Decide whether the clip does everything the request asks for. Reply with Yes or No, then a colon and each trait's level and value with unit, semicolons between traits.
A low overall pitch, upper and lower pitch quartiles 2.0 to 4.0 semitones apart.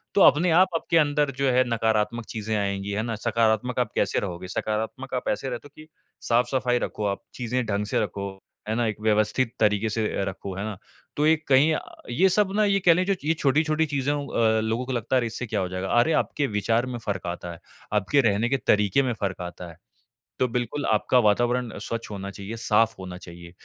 No: low, 115 Hz; average, 4.4 semitones